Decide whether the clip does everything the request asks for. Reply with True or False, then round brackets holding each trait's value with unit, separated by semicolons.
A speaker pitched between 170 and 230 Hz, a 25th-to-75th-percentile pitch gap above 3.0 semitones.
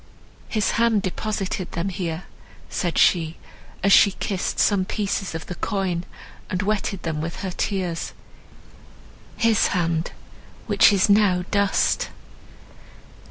False (190 Hz; 2.7 semitones)